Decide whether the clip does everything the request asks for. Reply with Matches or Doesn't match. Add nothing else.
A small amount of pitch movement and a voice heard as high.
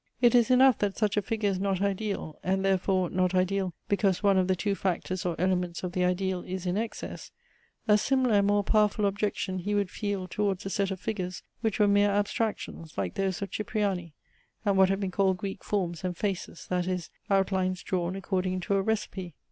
Matches